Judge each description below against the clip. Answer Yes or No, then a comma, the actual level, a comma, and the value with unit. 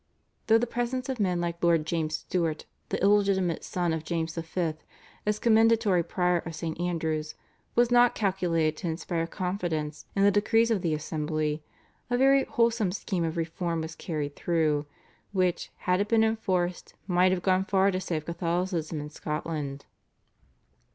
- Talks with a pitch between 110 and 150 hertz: No, medium, 175 Hz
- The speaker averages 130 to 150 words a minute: No, average, 160 wpm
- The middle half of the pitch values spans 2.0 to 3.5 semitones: No, average, 3.9 semitones